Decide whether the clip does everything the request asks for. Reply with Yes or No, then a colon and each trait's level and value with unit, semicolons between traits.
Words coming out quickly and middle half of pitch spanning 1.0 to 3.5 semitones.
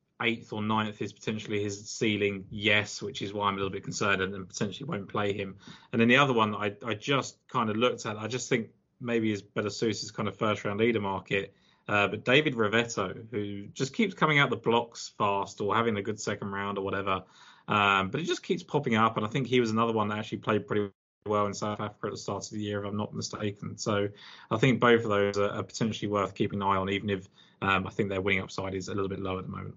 Yes: fast, 260 wpm; narrow, 2.5 semitones